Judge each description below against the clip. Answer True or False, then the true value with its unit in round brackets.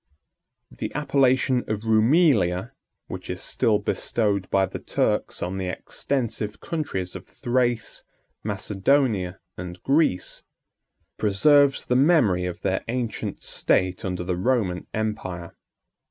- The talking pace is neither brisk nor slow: False (120 wpm)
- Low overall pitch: True (110 Hz)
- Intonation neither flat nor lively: False (5.7 semitones)